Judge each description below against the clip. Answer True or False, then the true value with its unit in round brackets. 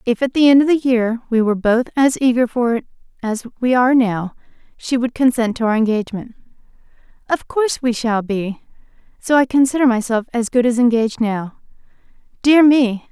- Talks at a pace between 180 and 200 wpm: True (185 wpm)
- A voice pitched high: True (240 Hz)